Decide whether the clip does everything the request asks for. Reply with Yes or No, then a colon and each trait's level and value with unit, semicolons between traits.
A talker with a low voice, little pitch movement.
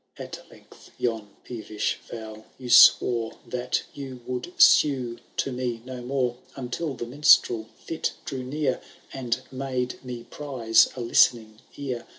Yes: low, 125 Hz; narrow, 2.1 semitones